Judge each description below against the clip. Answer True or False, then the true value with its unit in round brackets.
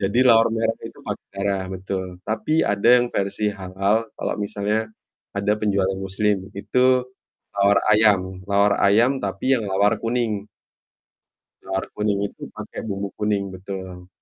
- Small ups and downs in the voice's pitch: True (1.5 semitones)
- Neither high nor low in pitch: False (100 Hz)